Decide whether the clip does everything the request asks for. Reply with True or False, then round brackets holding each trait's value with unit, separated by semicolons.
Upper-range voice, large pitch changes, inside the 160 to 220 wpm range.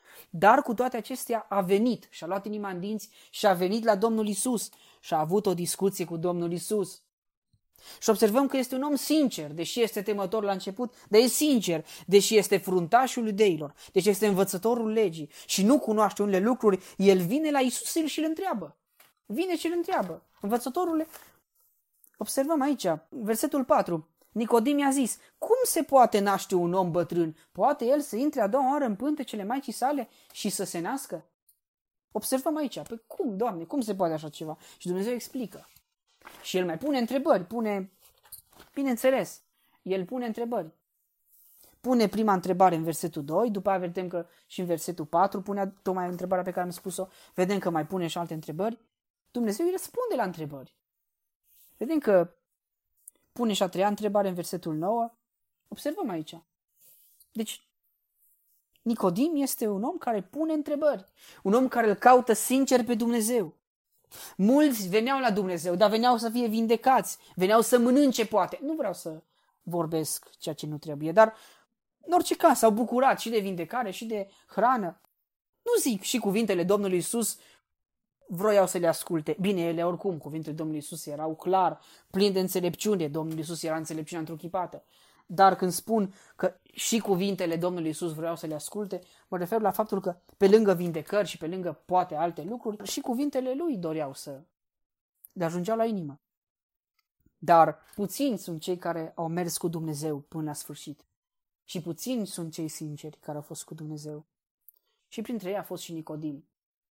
True (200 Hz; 5.9 semitones; 170 wpm)